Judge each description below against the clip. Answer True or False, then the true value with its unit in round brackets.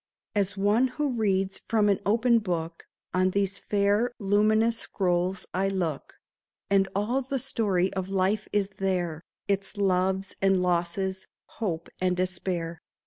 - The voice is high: True (195 Hz)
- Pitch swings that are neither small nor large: False (2.3 semitones)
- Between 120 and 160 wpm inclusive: True (140 wpm)